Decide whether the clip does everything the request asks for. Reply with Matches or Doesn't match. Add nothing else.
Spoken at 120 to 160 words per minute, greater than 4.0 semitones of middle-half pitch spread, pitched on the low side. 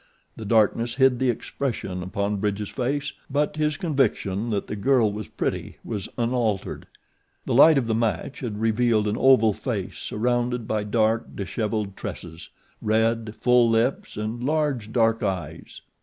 Doesn't match